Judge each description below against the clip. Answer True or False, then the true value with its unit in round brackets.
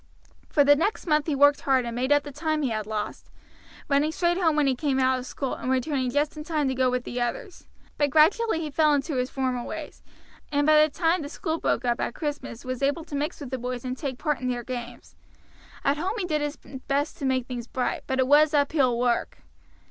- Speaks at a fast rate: True (245 wpm)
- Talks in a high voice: True (285 Hz)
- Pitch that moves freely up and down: False (3.2 semitones)